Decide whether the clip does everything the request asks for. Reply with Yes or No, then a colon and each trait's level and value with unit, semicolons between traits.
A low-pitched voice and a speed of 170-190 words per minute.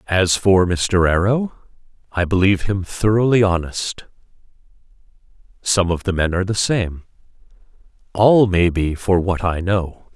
No: very low, 95 Hz; slow, 135 wpm